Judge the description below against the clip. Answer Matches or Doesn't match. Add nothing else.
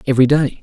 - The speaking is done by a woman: Doesn't match